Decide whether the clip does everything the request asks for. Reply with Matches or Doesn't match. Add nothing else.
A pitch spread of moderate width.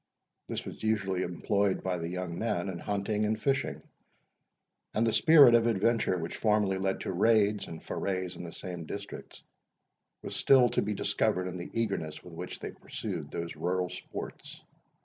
Matches